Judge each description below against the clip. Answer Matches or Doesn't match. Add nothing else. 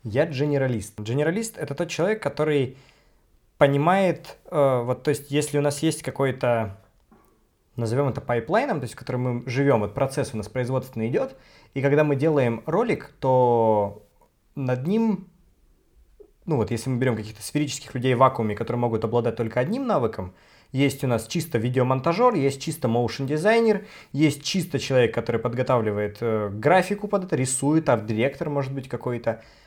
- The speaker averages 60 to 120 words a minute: Doesn't match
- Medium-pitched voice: Doesn't match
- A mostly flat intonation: Doesn't match